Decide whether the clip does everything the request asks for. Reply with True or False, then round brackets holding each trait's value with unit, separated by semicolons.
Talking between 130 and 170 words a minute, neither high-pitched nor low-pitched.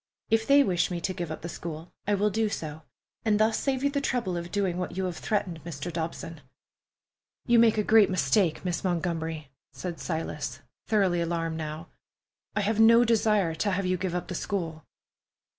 False (190 wpm; 180 Hz)